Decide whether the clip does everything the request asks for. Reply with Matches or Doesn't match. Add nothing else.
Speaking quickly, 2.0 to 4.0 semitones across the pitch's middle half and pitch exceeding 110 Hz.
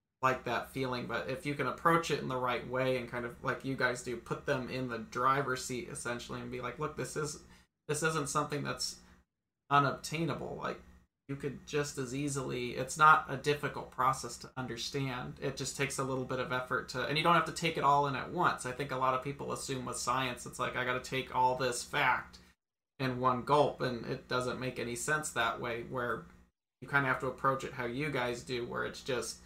Matches